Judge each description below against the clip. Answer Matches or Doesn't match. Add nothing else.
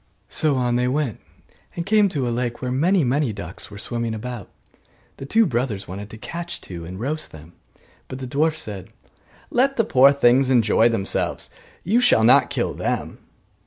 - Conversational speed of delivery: Matches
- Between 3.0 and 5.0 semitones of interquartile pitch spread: Doesn't match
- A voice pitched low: Matches